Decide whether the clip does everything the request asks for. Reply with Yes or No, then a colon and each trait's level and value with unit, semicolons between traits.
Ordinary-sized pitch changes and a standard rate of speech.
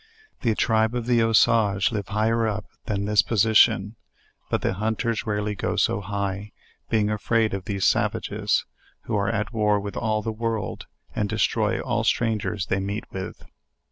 No: narrow, 1.9 semitones; average, 170 wpm